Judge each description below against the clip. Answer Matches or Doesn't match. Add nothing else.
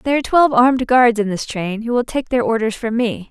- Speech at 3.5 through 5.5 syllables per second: Doesn't match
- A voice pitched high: Matches